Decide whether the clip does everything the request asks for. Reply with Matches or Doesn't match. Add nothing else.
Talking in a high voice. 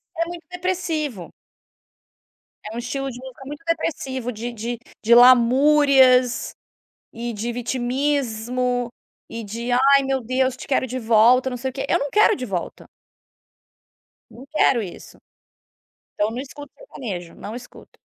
Matches